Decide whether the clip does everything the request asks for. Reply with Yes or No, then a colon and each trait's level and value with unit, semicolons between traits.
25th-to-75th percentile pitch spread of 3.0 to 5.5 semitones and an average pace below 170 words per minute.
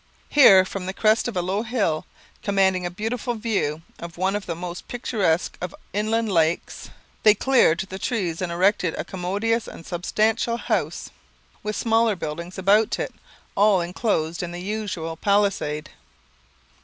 Yes: average, 3.8 semitones; average, 155 wpm